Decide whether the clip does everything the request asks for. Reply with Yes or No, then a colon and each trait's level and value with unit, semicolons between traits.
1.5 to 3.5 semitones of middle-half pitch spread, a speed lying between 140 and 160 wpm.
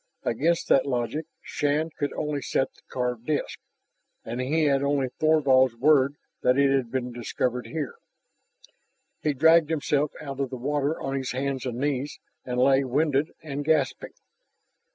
Yes: narrow, 2.6 semitones; average, 155 wpm